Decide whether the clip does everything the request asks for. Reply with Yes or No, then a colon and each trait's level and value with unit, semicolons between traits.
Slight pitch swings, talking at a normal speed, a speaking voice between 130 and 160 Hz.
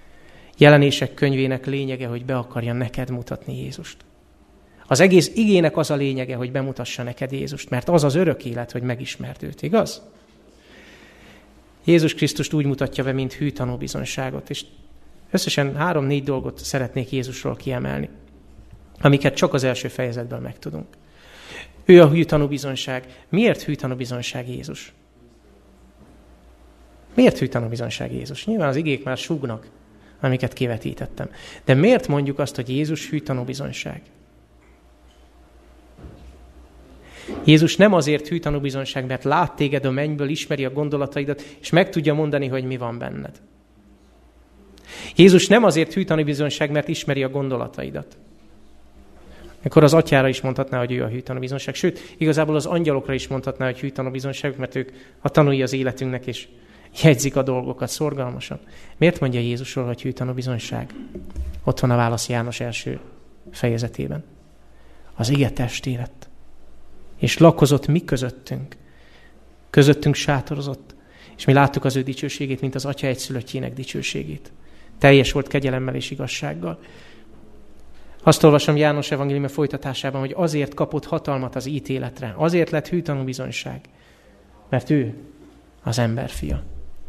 No: average, 3.4 semitones; average, 135 wpm; low, 135 Hz